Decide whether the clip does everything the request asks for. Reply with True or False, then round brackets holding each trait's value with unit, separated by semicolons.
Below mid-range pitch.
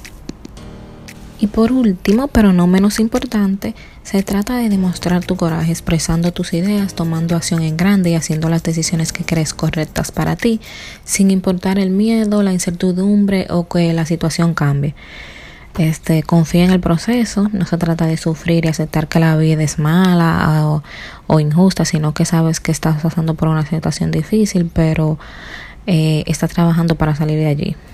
False (170 Hz)